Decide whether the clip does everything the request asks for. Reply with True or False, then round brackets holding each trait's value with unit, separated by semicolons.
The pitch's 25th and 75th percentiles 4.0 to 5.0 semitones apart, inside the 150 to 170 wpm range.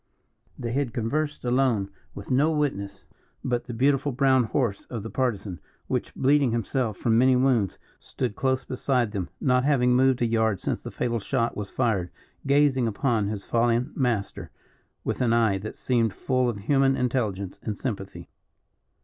False (3.4 semitones; 165 wpm)